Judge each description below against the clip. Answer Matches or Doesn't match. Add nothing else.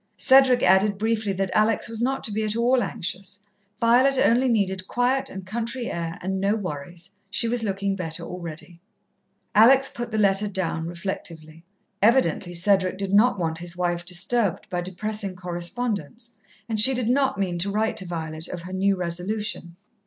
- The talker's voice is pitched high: Matches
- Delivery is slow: Doesn't match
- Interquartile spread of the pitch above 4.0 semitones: Matches